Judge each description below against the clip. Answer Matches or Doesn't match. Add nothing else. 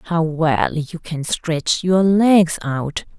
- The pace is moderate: Matches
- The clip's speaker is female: Matches